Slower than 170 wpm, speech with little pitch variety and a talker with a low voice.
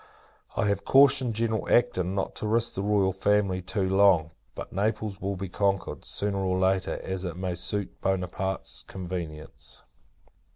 Yes: average, 155 wpm; narrow, 2.0 semitones; very low, 95 Hz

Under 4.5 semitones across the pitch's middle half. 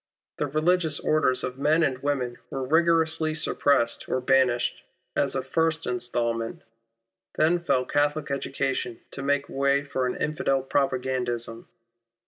Yes: average, 3.3 semitones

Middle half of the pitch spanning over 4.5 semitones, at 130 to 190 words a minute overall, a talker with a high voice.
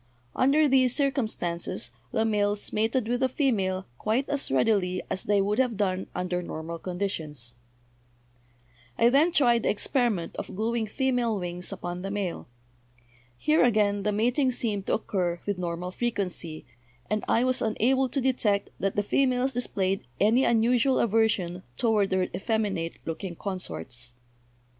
Yes: average, 4.9 semitones; average, 150 wpm; high, 210 Hz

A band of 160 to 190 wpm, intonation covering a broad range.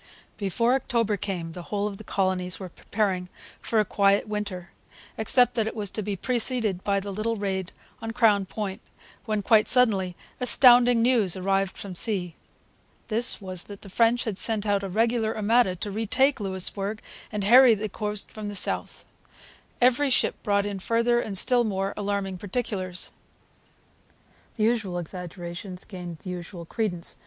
No: average, 165 wpm; average, 3.1 semitones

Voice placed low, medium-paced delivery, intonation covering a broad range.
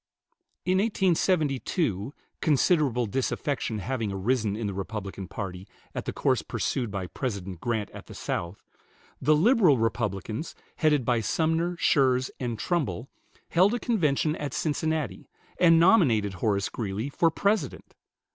No: low, 130 Hz; slow, 130 wpm; wide, 7.4 semitones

